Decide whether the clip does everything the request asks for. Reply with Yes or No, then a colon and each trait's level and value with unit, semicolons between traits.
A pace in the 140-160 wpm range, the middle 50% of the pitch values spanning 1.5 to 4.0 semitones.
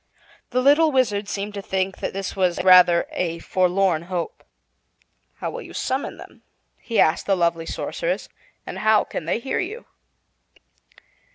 No: average, 155 wpm; average, 5.0 semitones